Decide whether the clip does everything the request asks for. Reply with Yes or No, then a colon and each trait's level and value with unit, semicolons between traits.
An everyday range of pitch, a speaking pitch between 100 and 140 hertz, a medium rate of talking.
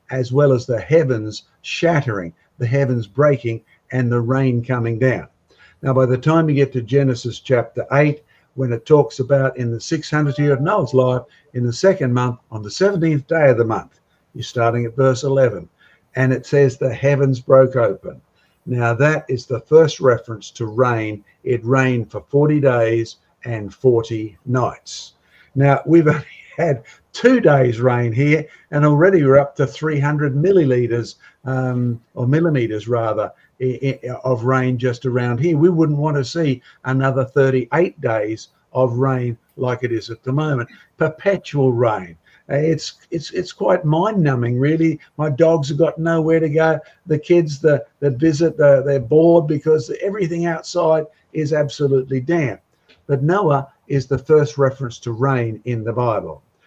Yes: average, 3.8 semitones; low, 135 Hz; average, 165 wpm